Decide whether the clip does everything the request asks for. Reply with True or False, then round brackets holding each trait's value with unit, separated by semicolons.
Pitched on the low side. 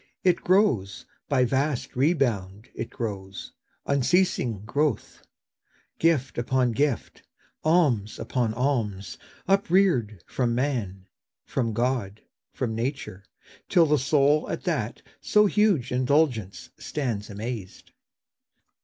True (125 Hz)